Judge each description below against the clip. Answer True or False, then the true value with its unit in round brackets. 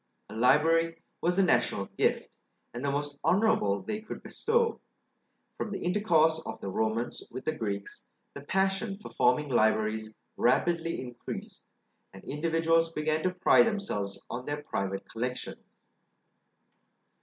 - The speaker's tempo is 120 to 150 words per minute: True (135 wpm)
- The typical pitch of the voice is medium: True (150 Hz)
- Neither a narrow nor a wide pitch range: False (7.3 semitones)